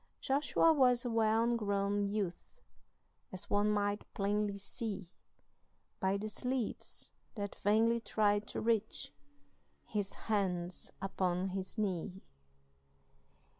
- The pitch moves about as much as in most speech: No, narrow, 2.3 semitones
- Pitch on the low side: No, high, 205 Hz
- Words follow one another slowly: Yes, slow, 105 wpm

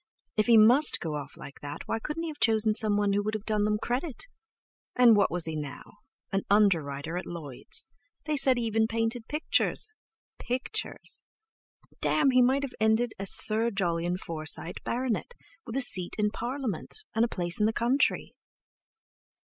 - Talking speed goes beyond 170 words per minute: No, average, 165 wpm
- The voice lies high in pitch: Yes, high, 220 Hz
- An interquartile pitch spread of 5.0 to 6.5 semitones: Yes, average, 5.3 semitones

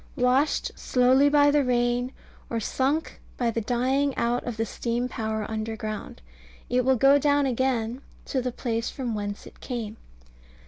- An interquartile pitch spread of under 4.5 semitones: Yes, average, 2.8 semitones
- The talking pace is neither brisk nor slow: Yes, average, 155 wpm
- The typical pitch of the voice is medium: No, high, 245 Hz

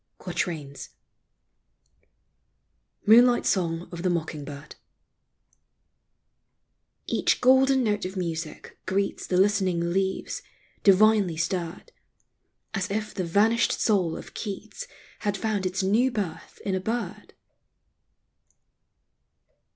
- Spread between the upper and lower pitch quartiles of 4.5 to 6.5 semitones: No, average, 3.8 semitones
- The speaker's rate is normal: No, slow, 100 wpm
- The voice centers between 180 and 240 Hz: Yes, high, 190 Hz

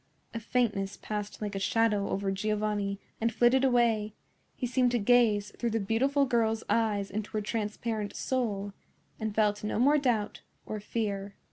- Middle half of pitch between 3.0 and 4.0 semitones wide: No, narrow, 2.4 semitones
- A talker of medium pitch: No, high, 215 Hz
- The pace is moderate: Yes, average, 160 wpm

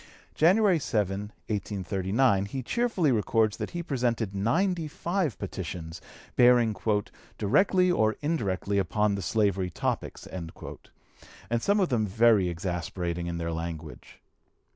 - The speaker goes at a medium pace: No, slow, 120 wpm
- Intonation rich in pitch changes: Yes, wide, 7.6 semitones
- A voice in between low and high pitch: No, low, 105 Hz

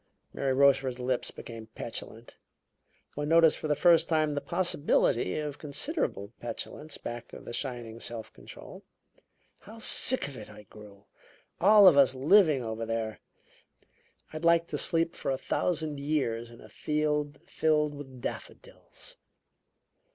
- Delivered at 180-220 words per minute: No, average, 145 wpm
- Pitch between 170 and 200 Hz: No, medium, 140 Hz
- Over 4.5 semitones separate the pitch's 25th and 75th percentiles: Yes, average, 4.9 semitones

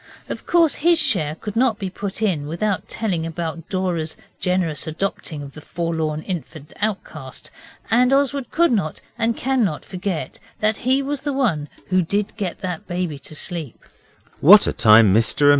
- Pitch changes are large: Yes, wide, 6.2 semitones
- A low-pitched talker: No, medium, 185 Hz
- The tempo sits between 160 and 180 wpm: No, average, 150 wpm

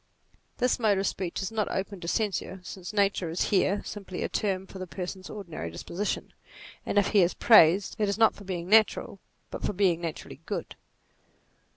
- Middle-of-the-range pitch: No, high, 195 Hz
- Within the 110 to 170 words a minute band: No, average, 190 wpm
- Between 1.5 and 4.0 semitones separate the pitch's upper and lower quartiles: Yes, narrow, 2.5 semitones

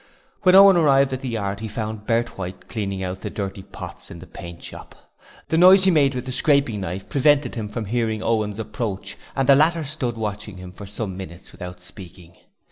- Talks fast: Yes, fast, 210 wpm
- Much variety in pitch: Yes, wide, 5.8 semitones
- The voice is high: No, low, 110 Hz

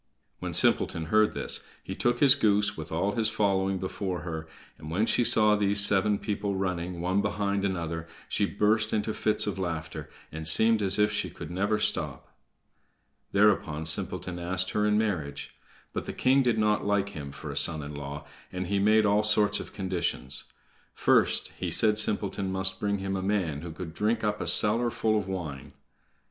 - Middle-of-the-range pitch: No, low, 100 Hz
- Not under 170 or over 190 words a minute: Yes, average, 185 wpm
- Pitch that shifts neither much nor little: Yes, average, 3.2 semitones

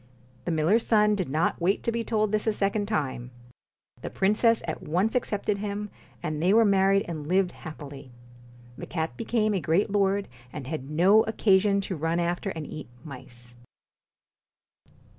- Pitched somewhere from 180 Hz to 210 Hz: Yes, high, 190 Hz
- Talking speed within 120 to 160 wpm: No, average, 170 wpm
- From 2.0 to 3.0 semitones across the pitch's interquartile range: No, average, 4.8 semitones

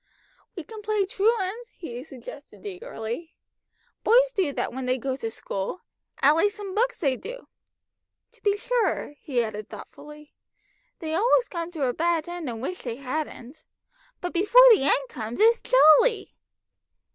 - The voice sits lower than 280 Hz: No, very high, 325 Hz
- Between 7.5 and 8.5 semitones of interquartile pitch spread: Yes, wide, 8.2 semitones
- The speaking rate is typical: Yes, average, 155 wpm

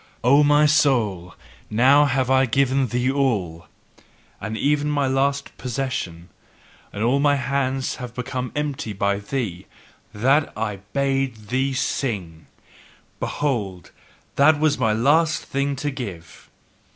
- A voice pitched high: No, low, 130 Hz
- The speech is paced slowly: Yes, slow, 125 wpm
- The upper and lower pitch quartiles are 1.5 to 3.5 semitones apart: No, average, 4.5 semitones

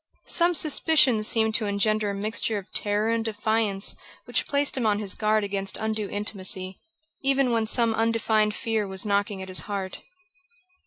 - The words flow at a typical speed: Yes, average, 165 wpm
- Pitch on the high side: Yes, high, 215 Hz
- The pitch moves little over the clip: Yes, narrow, 2.0 semitones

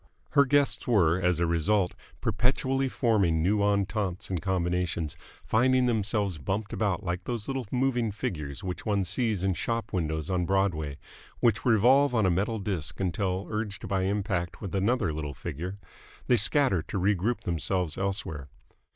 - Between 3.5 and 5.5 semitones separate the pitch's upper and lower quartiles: Yes, average, 4.1 semitones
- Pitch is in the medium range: No, very low, 95 Hz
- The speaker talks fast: No, average, 155 wpm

